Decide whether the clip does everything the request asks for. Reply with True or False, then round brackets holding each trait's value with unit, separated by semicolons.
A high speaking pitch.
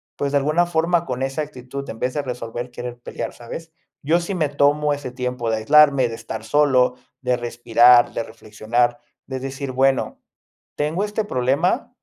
False (130 Hz)